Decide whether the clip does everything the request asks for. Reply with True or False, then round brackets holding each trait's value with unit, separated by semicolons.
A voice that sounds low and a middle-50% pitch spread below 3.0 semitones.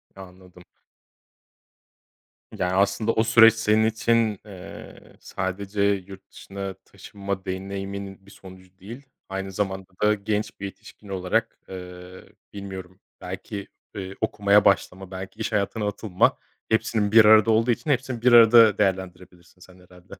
True (100 Hz; 2.4 semitones)